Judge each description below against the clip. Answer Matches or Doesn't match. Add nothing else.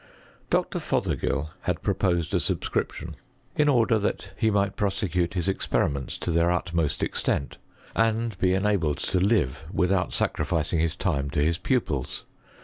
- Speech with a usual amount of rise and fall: Matches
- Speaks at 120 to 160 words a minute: Matches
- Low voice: Matches